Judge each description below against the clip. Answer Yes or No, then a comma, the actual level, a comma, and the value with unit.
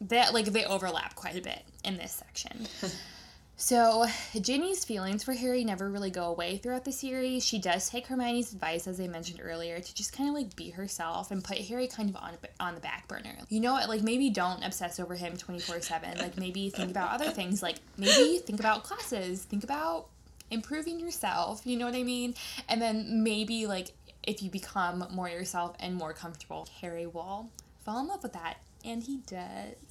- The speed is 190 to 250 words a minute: Yes, fast, 205 wpm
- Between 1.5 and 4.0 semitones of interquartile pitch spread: No, average, 5.2 semitones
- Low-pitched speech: No, high, 210 Hz